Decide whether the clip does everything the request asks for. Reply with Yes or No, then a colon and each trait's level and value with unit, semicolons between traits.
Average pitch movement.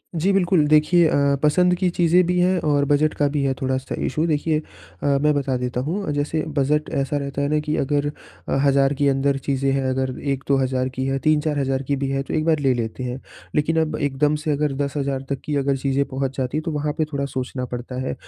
No: narrow, 2.1 semitones